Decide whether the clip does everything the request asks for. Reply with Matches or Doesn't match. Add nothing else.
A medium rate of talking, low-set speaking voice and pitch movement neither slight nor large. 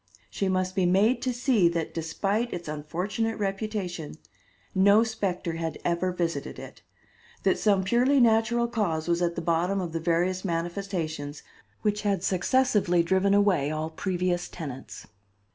Doesn't match